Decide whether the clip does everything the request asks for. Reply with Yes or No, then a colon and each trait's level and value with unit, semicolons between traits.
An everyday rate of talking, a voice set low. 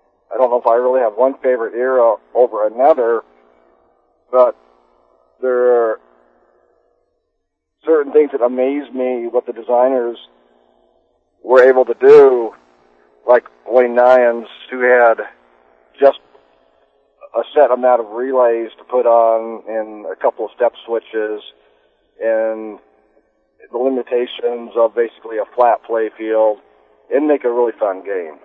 No: slow, 130 wpm; low, 115 Hz